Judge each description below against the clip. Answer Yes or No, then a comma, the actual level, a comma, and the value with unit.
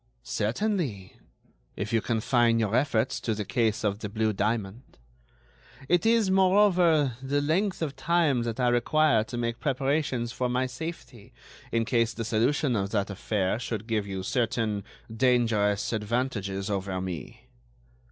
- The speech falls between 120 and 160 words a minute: Yes, average, 145 wpm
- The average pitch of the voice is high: No, low, 115 Hz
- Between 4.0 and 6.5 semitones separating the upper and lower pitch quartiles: Yes, average, 4.3 semitones